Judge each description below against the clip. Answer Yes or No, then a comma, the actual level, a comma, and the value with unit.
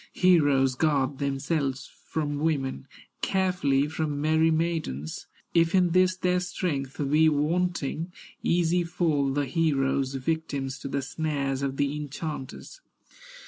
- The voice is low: No, medium, 150 Hz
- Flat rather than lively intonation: No, average, 3.3 semitones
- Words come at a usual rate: No, slow, 120 wpm